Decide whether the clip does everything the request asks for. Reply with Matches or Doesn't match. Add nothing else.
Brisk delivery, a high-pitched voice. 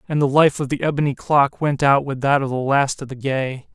Doesn't match